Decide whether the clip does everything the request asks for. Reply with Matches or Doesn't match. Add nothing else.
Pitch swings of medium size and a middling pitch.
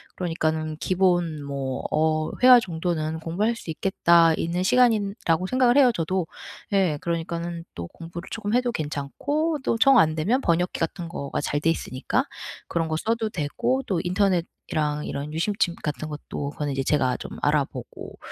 Matches